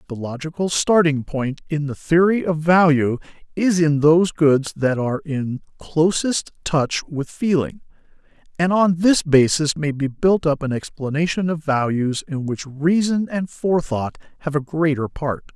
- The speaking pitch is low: No, medium, 155 Hz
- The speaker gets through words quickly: No, average, 160 wpm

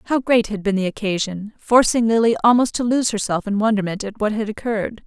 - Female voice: Yes, female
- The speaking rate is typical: No, fast, 215 wpm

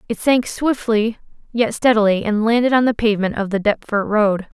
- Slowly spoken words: No, average, 185 wpm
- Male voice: No, female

